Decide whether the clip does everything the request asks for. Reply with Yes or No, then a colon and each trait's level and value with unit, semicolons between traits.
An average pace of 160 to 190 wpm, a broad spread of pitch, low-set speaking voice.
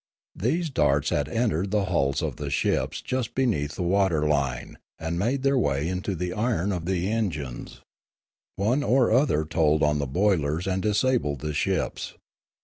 Yes: average, 170 wpm; wide, 6.8 semitones; very low, 90 Hz